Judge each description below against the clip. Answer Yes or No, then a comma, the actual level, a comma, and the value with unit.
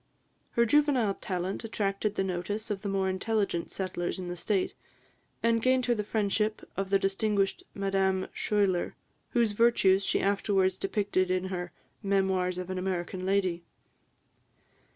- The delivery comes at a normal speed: Yes, average, 145 wpm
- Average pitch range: No, narrow, 2.1 semitones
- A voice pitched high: Yes, high, 195 Hz